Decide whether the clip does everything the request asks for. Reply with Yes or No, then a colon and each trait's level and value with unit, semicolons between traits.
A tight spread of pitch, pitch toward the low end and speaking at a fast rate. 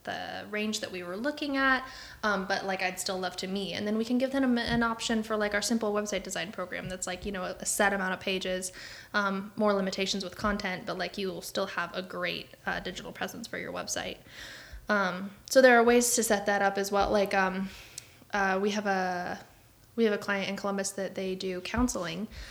No: narrow, 2.2 semitones; high, 200 Hz; fast, 225 wpm